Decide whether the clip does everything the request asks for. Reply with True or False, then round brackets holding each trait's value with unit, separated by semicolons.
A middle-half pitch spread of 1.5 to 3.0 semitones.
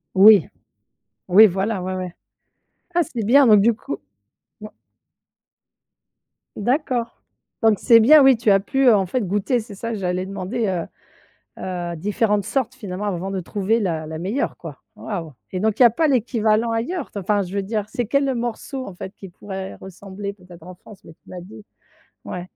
False (3.8 semitones)